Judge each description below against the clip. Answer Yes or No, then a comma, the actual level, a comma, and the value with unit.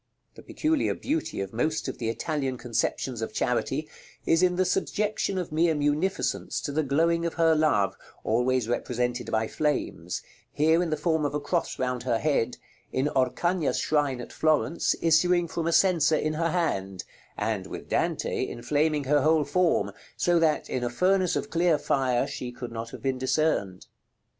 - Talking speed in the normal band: Yes, average, 175 wpm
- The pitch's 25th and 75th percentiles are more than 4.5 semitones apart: Yes, average, 5.1 semitones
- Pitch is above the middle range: No, medium, 150 Hz